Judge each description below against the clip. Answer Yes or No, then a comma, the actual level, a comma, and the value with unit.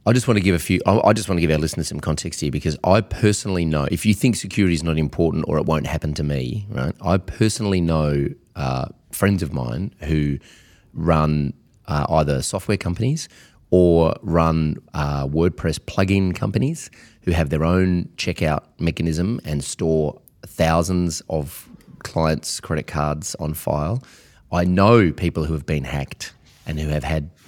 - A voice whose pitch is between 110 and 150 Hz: No, very low, 85 Hz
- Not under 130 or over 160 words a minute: No, average, 175 wpm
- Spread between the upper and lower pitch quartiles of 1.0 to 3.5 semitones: No, average, 4.1 semitones